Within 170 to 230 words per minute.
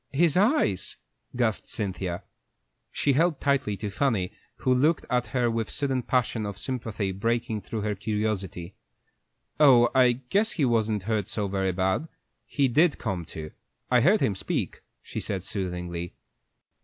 No: average, 155 wpm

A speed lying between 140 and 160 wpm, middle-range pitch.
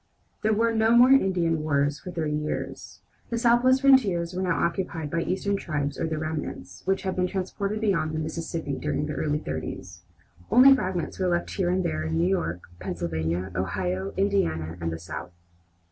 No: average, 180 wpm; medium, 165 Hz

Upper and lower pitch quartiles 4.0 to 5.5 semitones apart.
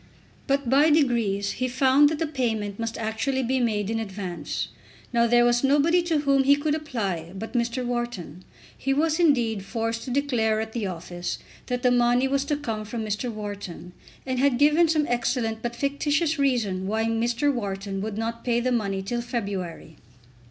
Yes: average, 4.3 semitones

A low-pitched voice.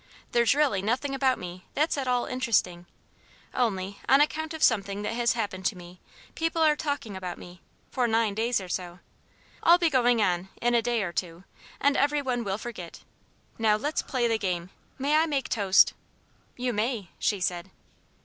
No: high, 230 Hz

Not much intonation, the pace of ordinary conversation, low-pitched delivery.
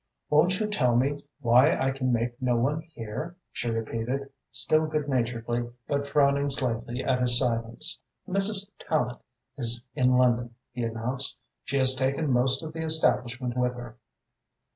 No: average, 3.0 semitones; average, 155 wpm; low, 125 Hz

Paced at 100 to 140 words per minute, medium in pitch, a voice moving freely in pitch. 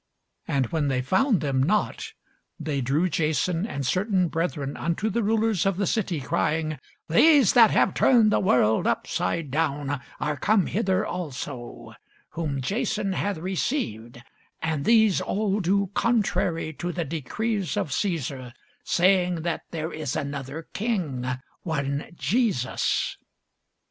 Yes: slow, 135 wpm; medium, 170 Hz; wide, 6.1 semitones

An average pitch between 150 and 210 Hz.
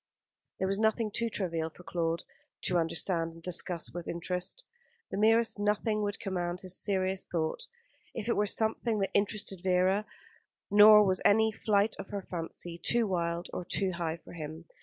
Yes: high, 190 Hz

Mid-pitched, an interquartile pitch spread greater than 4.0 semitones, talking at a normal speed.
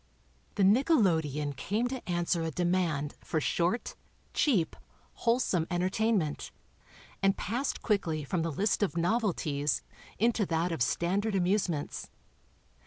No: medium, 180 Hz; average, 4.7 semitones; slow, 115 wpm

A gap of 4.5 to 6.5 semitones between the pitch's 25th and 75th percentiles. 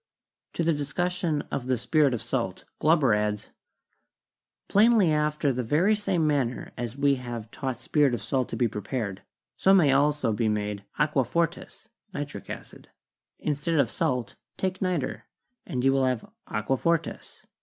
Yes: average, 5.0 semitones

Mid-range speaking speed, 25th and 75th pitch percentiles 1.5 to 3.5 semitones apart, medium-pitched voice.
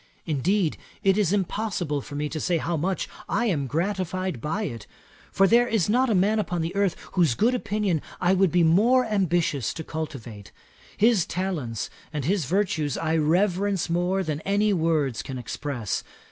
No: average, 170 wpm; average, 4.7 semitones; medium, 175 Hz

